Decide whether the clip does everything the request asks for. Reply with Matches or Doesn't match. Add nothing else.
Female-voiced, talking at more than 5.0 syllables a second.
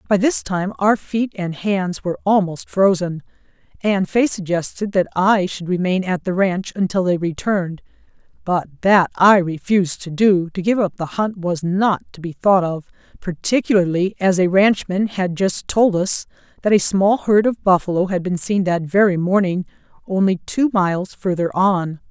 Doesn't match